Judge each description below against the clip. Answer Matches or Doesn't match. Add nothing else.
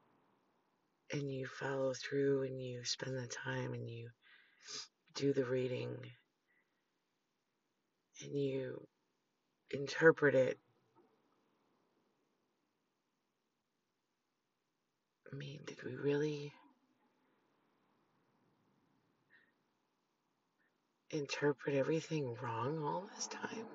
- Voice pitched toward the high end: Doesn't match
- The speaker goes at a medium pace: Doesn't match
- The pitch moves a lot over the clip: Doesn't match